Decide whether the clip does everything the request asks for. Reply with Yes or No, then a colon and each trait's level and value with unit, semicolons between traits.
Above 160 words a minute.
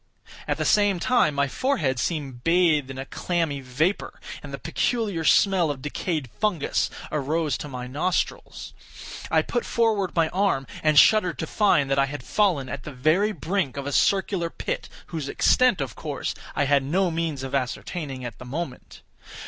Yes: average, 175 wpm